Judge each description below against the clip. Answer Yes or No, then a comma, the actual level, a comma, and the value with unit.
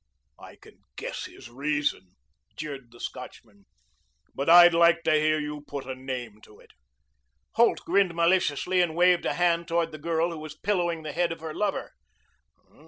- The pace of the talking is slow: No, average, 170 wpm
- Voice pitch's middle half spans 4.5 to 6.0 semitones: No, average, 3.4 semitones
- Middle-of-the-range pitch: Yes, medium, 160 Hz